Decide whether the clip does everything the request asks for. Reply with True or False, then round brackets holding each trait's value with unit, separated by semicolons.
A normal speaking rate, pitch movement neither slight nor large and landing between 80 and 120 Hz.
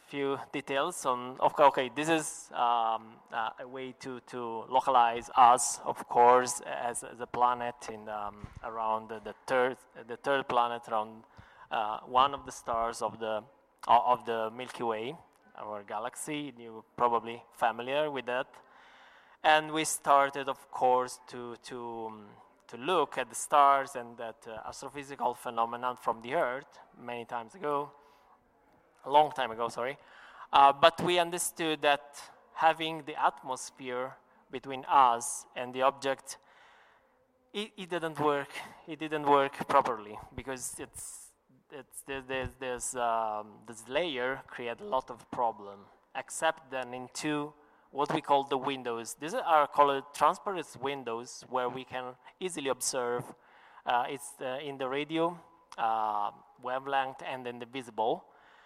False (145 wpm; 3.4 semitones; 130 Hz)